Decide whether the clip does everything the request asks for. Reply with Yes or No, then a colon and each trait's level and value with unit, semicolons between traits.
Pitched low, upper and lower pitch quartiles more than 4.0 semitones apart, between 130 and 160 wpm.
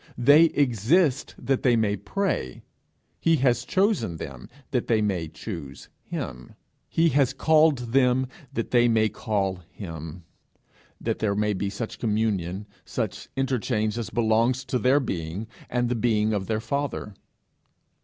Yes: low, 115 Hz; average, 4.6 semitones; average, 145 wpm